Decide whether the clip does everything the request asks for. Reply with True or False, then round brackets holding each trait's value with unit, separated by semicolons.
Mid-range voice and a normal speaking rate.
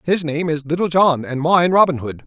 False (160 Hz; 240 wpm)